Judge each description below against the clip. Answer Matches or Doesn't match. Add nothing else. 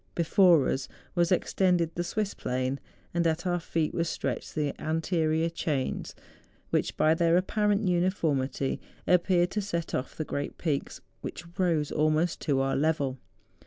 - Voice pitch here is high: Doesn't match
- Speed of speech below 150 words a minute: Doesn't match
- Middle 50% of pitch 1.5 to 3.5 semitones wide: Matches